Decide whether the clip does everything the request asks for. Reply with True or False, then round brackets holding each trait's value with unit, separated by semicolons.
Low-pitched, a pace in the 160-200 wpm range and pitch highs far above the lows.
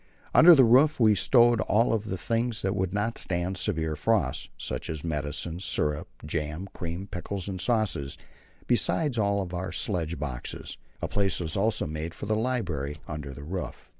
True (95 Hz; 165 wpm; 5.8 semitones)